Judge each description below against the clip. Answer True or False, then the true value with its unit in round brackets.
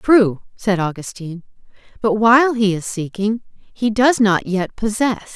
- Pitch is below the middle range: False (210 Hz)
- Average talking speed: True (145 wpm)